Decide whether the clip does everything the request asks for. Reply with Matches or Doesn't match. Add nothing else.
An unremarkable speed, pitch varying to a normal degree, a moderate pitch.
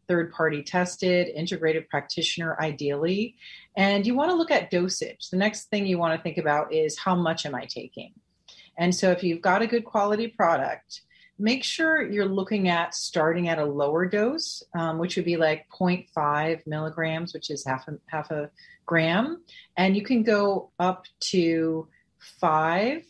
Matches